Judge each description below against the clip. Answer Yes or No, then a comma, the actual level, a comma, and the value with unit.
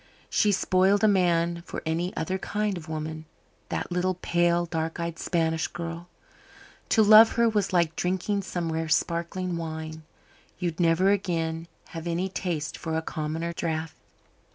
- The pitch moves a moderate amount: No, narrow, 2.3 semitones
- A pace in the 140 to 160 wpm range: Yes, average, 155 wpm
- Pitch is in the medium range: Yes, medium, 170 Hz